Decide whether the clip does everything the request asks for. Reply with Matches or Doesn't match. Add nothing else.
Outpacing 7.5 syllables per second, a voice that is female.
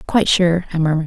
Matches